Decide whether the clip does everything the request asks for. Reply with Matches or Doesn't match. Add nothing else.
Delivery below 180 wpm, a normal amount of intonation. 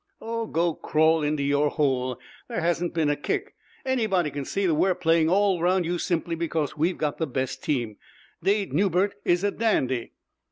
Doesn't match